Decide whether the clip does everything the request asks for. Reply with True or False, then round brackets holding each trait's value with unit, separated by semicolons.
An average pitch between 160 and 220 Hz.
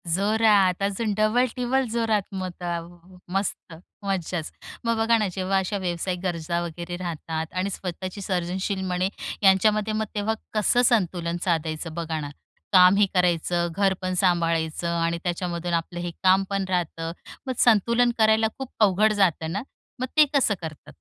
True (185 Hz)